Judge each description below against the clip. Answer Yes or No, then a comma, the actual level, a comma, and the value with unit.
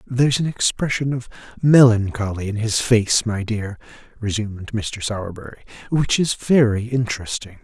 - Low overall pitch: Yes, low, 115 Hz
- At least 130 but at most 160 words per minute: Yes, slow, 135 wpm